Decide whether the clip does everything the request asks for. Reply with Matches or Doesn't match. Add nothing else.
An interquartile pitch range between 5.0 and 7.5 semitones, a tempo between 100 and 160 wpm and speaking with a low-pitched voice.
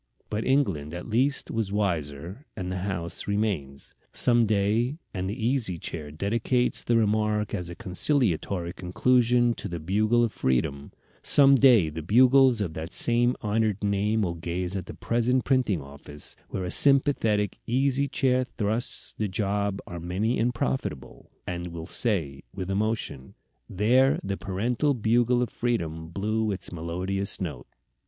Matches